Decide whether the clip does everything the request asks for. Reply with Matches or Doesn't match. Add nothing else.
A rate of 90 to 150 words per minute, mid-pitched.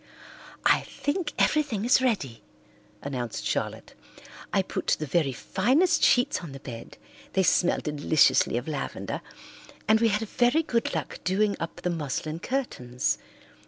Matches